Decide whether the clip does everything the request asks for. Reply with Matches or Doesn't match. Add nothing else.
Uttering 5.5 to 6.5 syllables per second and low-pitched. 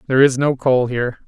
Doesn't match